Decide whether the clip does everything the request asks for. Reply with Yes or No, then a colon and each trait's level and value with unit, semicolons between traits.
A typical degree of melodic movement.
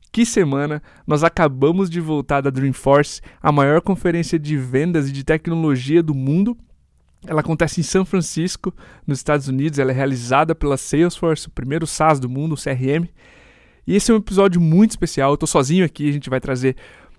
Yes: average, 3.4 semitones